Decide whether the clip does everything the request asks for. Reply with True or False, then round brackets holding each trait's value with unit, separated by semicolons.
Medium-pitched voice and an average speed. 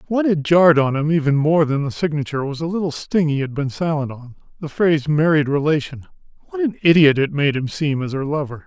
False (155 Hz; 215 wpm)